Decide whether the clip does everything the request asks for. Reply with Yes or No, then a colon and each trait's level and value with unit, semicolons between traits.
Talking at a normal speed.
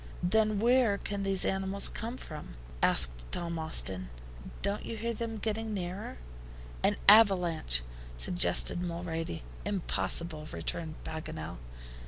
No: slow, 115 wpm